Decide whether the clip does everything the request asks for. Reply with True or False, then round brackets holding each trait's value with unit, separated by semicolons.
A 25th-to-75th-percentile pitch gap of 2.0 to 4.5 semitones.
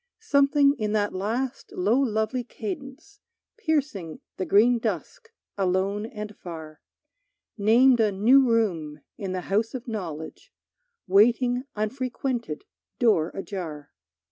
False (5.1 semitones)